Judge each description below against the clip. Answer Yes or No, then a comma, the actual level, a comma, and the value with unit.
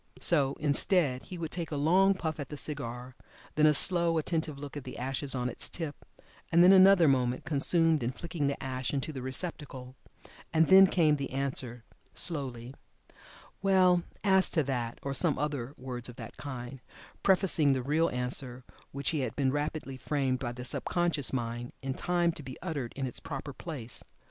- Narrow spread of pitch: No, average, 4.2 semitones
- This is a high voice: No, medium, 140 Hz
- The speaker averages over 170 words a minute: Yes, average, 185 wpm